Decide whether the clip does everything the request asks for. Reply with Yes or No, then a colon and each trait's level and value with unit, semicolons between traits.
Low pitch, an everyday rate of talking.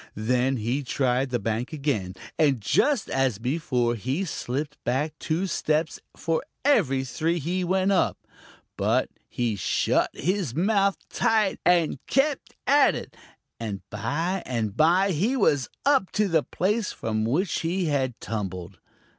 No: medium, 150 Hz; average, 145 wpm